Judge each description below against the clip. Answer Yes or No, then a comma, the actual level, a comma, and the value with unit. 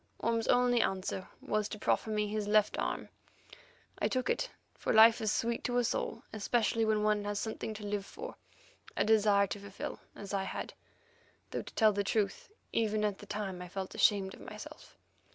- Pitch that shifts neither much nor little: No, narrow, 1.7 semitones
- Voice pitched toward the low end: No, high, 210 Hz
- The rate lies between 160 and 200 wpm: Yes, average, 190 wpm